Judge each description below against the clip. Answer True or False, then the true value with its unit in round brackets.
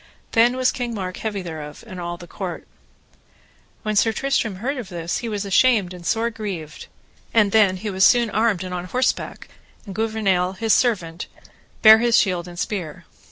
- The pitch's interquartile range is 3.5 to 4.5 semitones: True (3.9 semitones)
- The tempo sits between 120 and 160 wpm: False (180 wpm)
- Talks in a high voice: True (205 Hz)